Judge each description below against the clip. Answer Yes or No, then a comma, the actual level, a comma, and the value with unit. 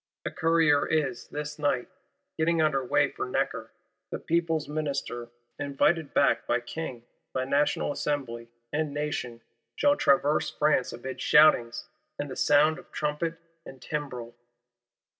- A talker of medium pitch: Yes, medium, 145 Hz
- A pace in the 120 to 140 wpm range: Yes, slow, 135 wpm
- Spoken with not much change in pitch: No, average, 3.0 semitones